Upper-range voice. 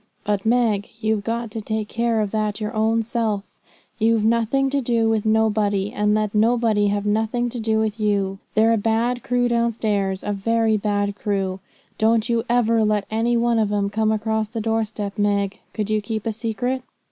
Yes: high, 220 Hz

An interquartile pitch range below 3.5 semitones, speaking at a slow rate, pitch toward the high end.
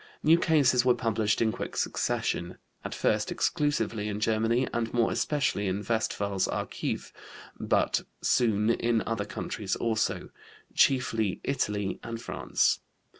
No: average, 2.9 semitones; slow, 125 wpm; low, 115 Hz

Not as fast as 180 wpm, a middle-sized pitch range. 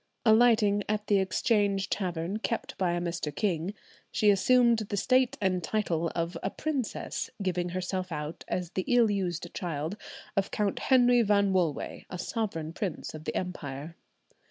Yes: average, 155 wpm; average, 3.6 semitones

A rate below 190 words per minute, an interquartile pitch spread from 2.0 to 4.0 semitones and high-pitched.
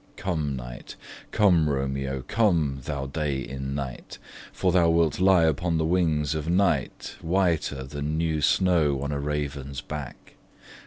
No: average, 145 wpm; average, 3.5 semitones; very low, 75 Hz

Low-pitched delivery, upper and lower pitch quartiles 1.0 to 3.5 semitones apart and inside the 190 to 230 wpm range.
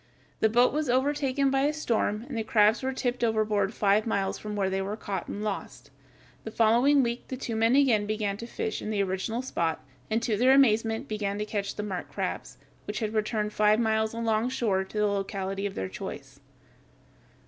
No: high, 220 Hz; average, 2.8 semitones; average, 200 wpm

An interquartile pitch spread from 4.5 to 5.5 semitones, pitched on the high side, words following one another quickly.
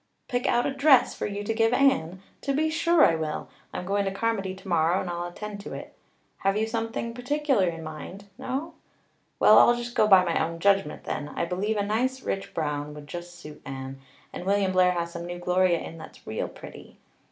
Yes: average, 5.2 semitones; high, 195 Hz; fast, 210 wpm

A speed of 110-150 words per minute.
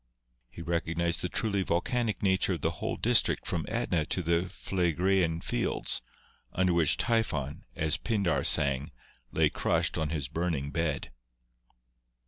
Yes: slow, 135 wpm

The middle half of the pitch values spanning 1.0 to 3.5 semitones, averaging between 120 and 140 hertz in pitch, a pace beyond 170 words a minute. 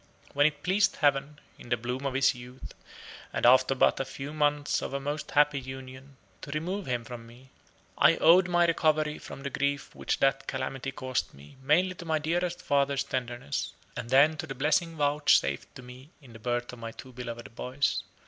Yes: average, 3.2 semitones; low, 135 Hz; average, 195 wpm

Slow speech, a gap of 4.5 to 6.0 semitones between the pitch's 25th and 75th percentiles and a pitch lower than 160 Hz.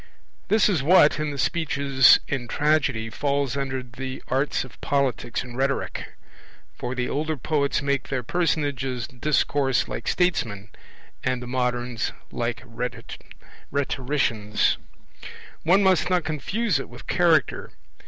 No: slow, 125 wpm; average, 3.5 semitones; low, 135 Hz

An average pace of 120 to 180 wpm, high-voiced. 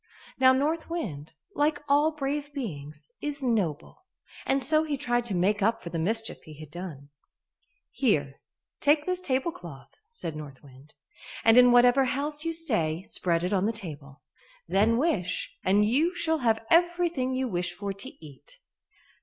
Yes: average, 160 wpm; high, 230 Hz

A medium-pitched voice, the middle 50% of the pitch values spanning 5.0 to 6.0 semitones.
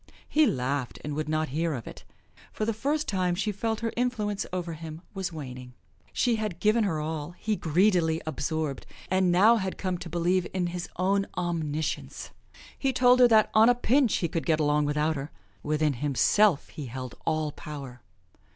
Yes: medium, 170 Hz; wide, 5.6 semitones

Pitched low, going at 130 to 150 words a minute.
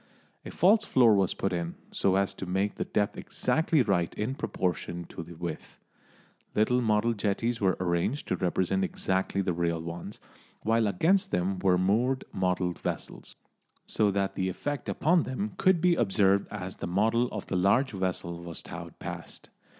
No: low, 100 Hz; average, 170 wpm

